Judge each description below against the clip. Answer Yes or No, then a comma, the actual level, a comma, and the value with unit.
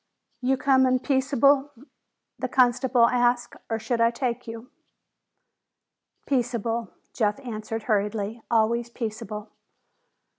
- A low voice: No, high, 235 Hz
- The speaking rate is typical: No, slow, 100 wpm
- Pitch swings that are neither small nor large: No, narrow, 2.3 semitones